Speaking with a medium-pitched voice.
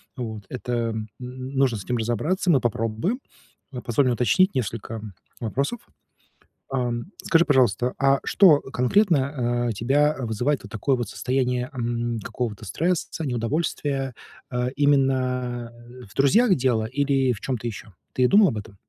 No: low, 125 Hz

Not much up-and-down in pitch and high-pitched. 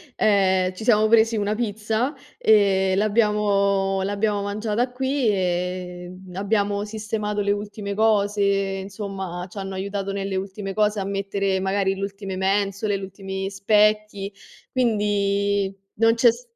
Yes: narrow, 1.7 semitones; high, 200 Hz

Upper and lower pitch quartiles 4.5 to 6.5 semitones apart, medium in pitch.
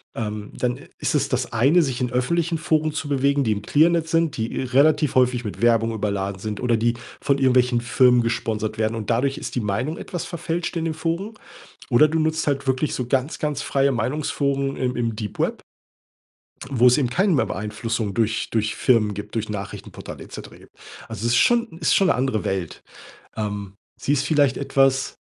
No: average, 4.9 semitones; low, 125 Hz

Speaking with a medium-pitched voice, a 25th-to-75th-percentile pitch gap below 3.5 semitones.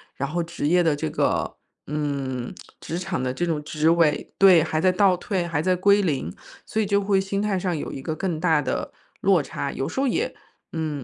No: medium, 170 Hz; average, 4.2 semitones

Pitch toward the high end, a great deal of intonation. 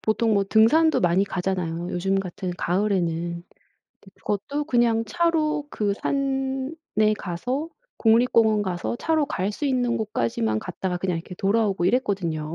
Yes: high, 210 Hz; wide, 6.3 semitones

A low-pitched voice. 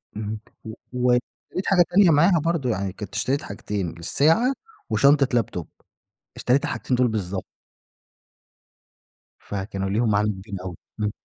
Yes: low, 110 Hz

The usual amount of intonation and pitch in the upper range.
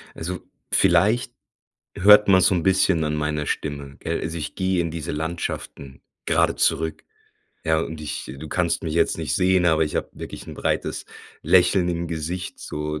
No: average, 3.1 semitones; very low, 80 Hz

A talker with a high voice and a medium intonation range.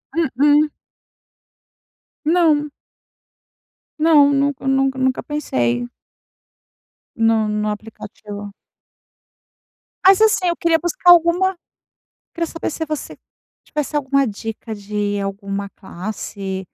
No: very high, 270 Hz; wide, 7.4 semitones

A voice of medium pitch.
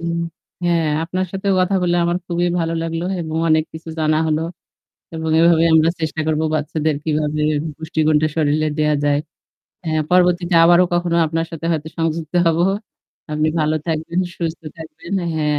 Yes: medium, 160 Hz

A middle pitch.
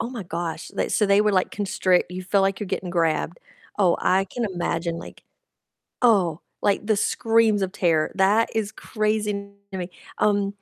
No: high, 195 Hz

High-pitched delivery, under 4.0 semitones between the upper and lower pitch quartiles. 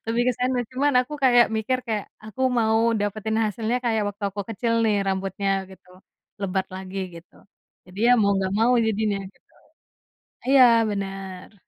Yes: high, 215 Hz; average, 3.2 semitones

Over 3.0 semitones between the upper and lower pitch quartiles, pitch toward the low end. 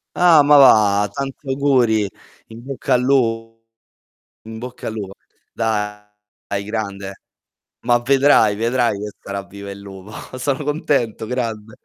Yes: average, 4.2 semitones; low, 115 Hz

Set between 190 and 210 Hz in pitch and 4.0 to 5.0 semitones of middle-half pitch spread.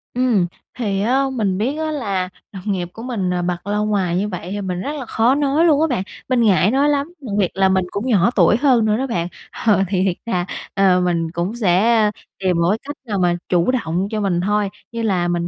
Yes: high, 205 Hz; average, 4.7 semitones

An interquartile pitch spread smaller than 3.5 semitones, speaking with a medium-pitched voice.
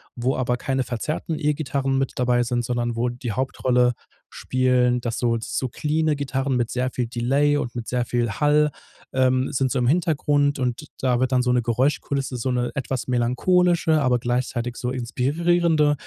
No: average, 2.7 semitones; low, 130 Hz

